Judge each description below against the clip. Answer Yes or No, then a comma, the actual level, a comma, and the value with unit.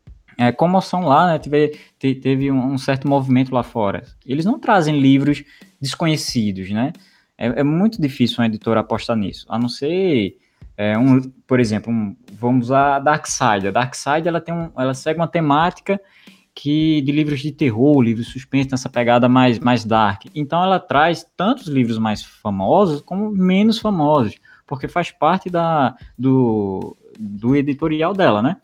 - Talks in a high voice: No, low, 135 Hz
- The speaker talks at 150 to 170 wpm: Yes, average, 160 wpm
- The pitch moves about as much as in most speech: Yes, average, 5.0 semitones